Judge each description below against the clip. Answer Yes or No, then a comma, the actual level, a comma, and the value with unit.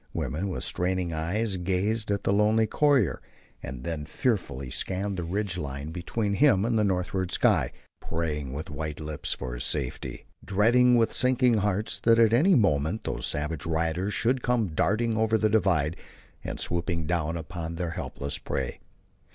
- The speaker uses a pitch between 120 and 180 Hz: No, very low, 95 Hz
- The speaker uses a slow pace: No, average, 165 wpm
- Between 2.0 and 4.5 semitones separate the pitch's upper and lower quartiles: No, wide, 5.5 semitones